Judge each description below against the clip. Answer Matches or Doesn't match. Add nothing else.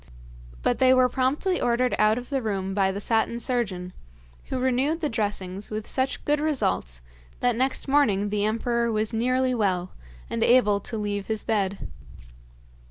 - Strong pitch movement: Doesn't match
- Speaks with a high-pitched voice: Matches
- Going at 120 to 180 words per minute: Matches